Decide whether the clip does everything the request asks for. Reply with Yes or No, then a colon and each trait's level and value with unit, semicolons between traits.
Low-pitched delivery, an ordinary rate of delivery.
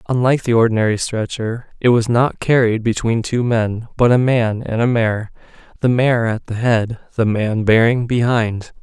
Yes: low, 115 Hz; average, 170 wpm